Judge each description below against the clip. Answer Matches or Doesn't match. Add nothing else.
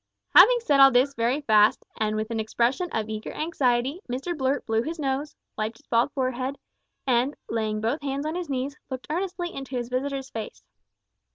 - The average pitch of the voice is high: Matches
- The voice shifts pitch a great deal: Doesn't match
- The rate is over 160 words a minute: Matches